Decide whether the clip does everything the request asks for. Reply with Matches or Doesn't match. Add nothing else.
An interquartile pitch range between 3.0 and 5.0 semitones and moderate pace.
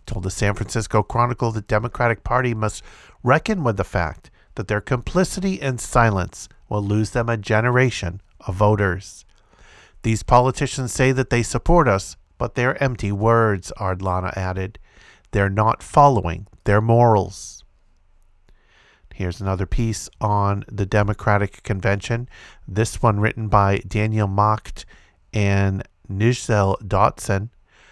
Doesn't match